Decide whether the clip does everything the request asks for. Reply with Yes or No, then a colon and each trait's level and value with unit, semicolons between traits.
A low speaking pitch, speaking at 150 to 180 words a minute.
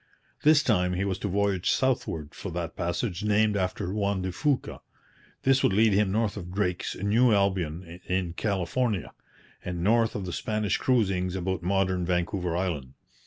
Yes: very low, 95 Hz; average, 165 wpm